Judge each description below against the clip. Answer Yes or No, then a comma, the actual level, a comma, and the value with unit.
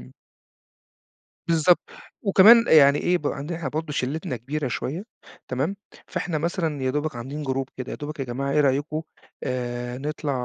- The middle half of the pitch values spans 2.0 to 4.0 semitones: Yes, average, 3.4 semitones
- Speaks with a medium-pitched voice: Yes, medium, 145 Hz